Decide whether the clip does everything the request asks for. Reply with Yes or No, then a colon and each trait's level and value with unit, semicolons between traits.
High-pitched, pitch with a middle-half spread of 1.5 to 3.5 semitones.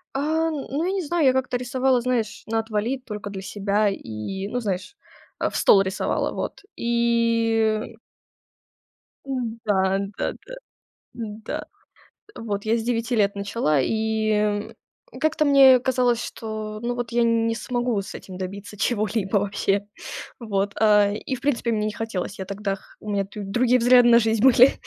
Yes: high, 225 Hz; average, 3.2 semitones